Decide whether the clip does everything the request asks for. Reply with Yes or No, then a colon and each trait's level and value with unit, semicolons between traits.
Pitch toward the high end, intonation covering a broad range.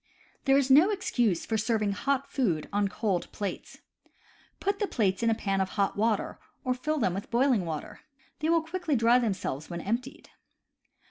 Yes: high, 230 Hz; wide, 5.8 semitones